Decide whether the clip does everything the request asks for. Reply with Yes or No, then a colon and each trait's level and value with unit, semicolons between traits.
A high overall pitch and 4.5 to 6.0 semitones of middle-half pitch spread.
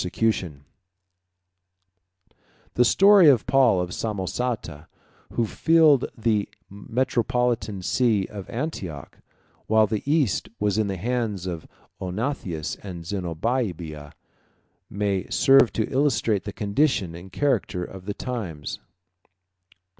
No: low, 105 Hz; average, 5.2 semitones